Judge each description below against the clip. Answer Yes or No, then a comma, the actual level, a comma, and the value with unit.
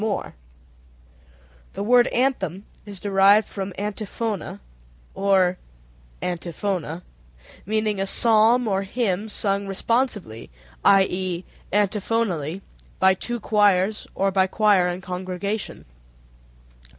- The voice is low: No, high, 195 Hz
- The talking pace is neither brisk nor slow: No, slow, 95 wpm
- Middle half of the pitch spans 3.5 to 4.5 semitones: No, average, 2.8 semitones